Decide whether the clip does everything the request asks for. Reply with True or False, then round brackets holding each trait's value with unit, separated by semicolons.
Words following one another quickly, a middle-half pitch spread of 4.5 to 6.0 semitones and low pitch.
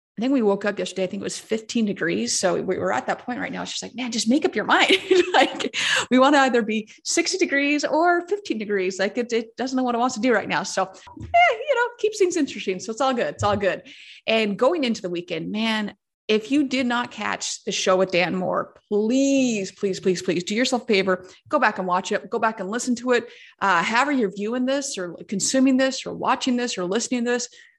False (250 wpm; 4.9 semitones; 240 Hz)